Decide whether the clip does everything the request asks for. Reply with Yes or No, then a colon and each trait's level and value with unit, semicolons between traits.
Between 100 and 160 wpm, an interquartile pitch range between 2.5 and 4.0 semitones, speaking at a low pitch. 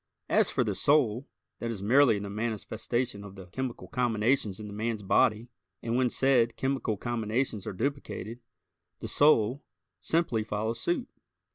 Yes: average, 150 wpm; average, 3.6 semitones; low, 115 Hz